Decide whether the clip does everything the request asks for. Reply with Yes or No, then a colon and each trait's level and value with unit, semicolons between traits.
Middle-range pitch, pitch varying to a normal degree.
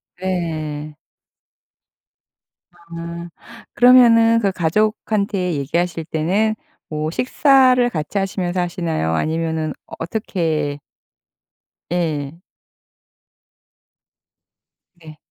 Yes: medium, 170 Hz; average, 4.5 semitones